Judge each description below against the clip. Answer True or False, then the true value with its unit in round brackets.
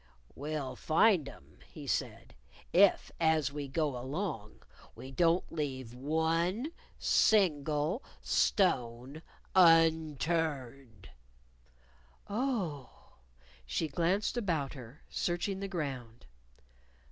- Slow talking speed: True (90 wpm)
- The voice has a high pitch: False (155 Hz)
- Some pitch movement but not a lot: True (4.5 semitones)